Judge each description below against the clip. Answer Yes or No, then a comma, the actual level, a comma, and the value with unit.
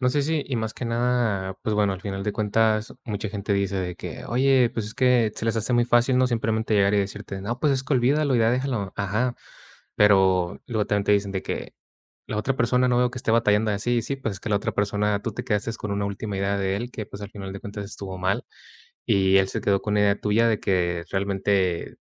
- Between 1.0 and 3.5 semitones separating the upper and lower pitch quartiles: Yes, average, 3.2 semitones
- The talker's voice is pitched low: Yes, low, 105 Hz